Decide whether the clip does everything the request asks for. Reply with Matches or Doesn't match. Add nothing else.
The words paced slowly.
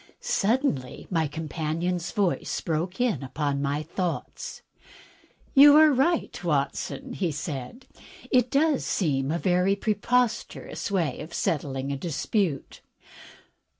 Matches